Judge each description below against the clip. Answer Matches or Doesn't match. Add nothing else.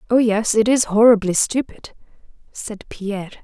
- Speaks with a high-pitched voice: Matches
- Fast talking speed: Doesn't match